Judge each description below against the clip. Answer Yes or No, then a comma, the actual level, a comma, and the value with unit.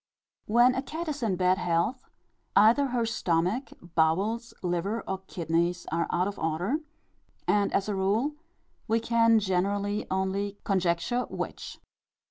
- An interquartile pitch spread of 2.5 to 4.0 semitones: No, average, 4.5 semitones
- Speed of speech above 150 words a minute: No, slow, 135 wpm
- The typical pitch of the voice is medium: No, high, 200 Hz